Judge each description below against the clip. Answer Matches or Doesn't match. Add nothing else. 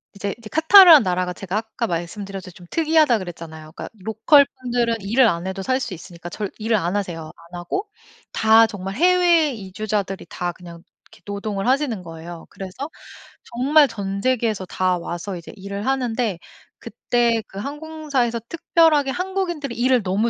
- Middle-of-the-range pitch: Doesn't match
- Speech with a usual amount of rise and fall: Doesn't match